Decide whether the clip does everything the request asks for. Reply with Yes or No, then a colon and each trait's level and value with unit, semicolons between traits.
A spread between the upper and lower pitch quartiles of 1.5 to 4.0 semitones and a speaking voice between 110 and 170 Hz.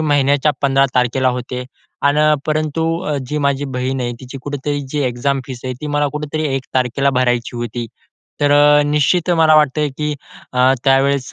Yes: narrow, 2.5 semitones; medium, 140 Hz